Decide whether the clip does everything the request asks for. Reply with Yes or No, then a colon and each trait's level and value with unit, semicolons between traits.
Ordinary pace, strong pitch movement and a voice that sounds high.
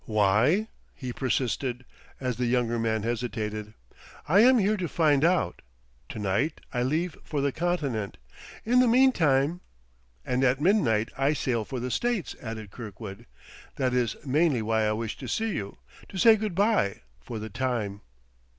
No: average, 165 wpm; wide, 7.2 semitones; low, 125 Hz